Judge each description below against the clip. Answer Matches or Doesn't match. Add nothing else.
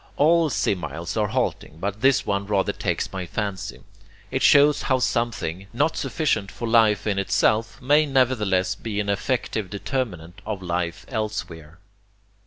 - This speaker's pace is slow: Doesn't match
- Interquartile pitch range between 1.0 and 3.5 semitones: Doesn't match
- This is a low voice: Matches